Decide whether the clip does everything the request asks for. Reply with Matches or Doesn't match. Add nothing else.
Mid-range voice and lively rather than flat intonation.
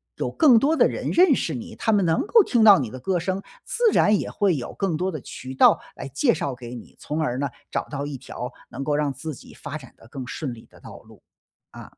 Matches